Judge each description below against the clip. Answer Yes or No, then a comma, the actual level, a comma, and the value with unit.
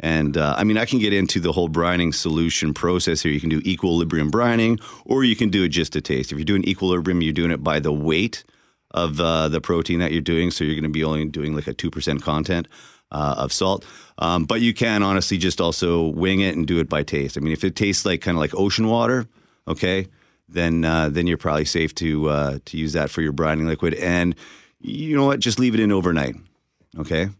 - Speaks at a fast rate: Yes, fast, 240 wpm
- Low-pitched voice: Yes, very low, 85 Hz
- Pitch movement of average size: Yes, average, 3.4 semitones